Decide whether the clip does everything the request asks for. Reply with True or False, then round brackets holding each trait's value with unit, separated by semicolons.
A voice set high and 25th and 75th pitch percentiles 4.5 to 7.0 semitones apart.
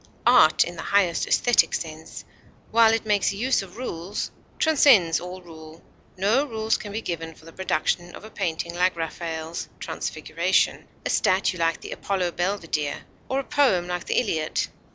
False (180 Hz; 4.8 semitones)